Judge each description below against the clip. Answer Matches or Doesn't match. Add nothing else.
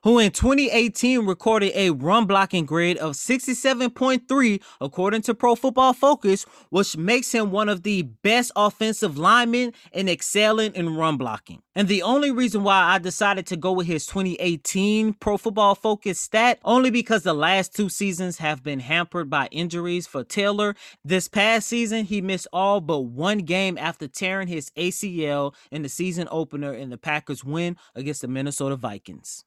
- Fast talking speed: Doesn't match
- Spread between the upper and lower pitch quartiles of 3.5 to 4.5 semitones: Doesn't match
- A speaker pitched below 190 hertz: Doesn't match